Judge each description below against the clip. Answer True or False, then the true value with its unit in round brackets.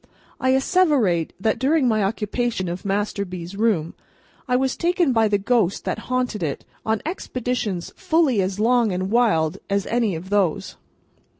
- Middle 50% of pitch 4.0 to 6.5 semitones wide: True (4.8 semitones)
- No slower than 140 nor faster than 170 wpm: True (160 wpm)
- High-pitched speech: True (220 Hz)